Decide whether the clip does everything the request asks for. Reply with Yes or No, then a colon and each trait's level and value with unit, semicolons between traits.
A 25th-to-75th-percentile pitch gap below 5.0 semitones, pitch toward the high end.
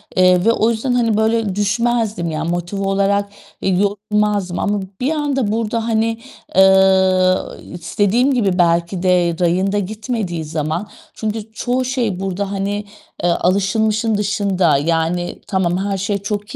Yes: average, 3.2 semitones; high, 200 Hz